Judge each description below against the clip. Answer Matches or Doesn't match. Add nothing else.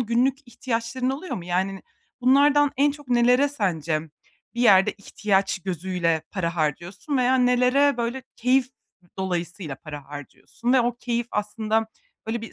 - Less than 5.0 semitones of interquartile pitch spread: Doesn't match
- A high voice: Matches